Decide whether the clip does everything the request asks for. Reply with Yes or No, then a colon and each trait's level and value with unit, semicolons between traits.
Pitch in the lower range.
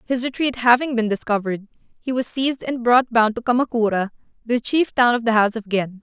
No: high, 235 Hz